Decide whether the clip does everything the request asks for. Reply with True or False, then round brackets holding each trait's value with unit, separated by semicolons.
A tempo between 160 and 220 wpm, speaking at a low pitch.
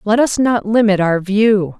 False (200 wpm; 210 Hz)